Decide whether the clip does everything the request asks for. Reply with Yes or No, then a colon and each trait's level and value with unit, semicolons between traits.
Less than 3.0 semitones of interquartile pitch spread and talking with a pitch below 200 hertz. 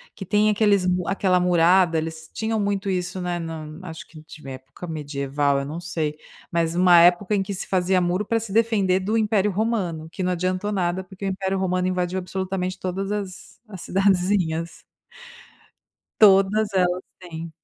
Yes: narrow, 2.6 semitones; medium, 185 Hz